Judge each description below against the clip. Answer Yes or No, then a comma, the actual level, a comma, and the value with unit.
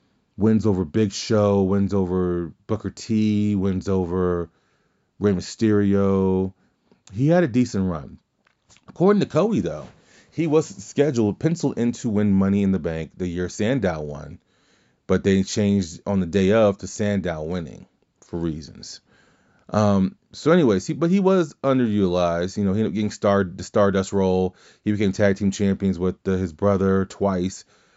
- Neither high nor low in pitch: No, low, 100 Hz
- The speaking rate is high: No, average, 165 wpm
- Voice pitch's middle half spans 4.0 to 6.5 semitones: No, narrow, 2.5 semitones